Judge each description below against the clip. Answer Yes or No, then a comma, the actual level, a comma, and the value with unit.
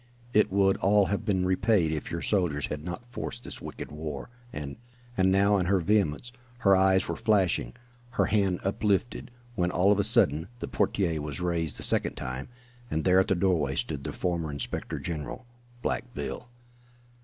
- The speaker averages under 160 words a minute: No, average, 185 wpm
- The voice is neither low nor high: No, very low, 95 Hz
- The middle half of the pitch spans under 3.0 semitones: No, average, 4.1 semitones